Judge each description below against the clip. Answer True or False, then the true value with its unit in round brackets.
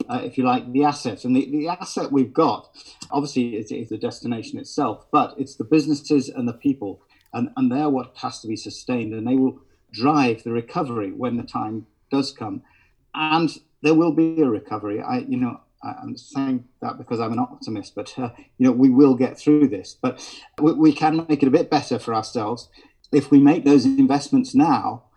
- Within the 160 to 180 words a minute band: False (205 wpm)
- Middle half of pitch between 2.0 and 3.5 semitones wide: False (5.4 semitones)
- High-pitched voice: False (145 Hz)